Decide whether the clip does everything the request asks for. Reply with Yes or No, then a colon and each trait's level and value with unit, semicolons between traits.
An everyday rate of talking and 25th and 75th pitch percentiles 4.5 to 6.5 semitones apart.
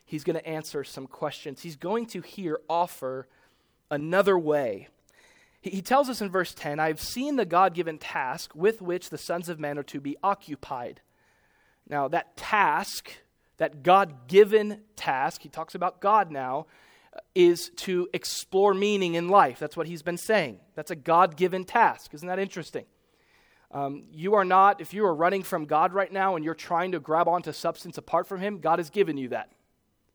No: average, 180 wpm; average, 4.1 semitones